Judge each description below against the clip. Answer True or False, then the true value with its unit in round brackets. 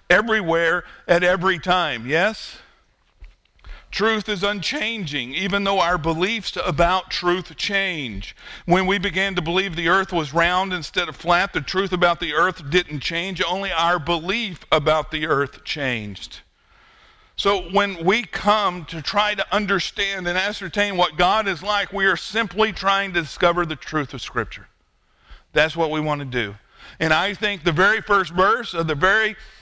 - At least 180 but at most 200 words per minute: False (165 wpm)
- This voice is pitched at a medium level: True (180 Hz)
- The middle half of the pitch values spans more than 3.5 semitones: False (3.2 semitones)